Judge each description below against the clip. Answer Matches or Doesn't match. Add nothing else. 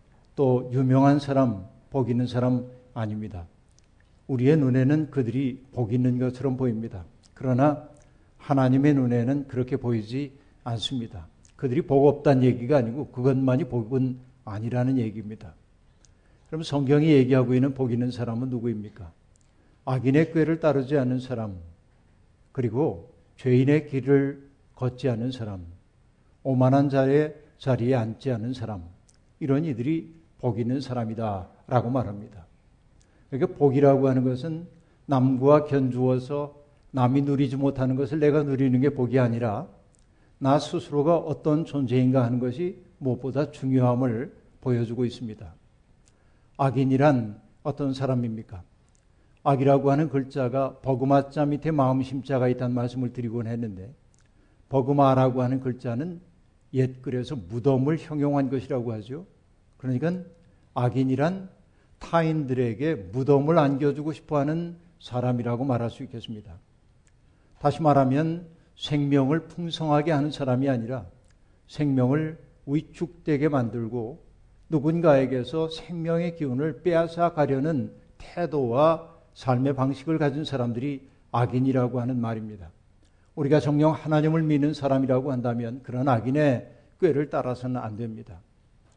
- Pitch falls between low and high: Doesn't match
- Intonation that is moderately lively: Matches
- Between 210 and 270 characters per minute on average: Doesn't match